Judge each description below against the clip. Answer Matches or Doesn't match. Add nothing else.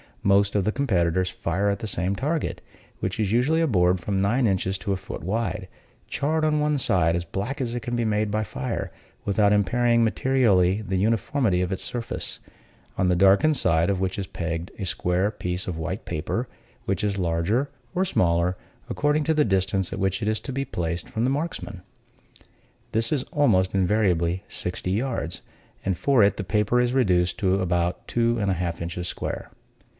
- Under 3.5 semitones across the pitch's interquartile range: Doesn't match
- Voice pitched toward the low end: Matches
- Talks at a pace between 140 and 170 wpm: Doesn't match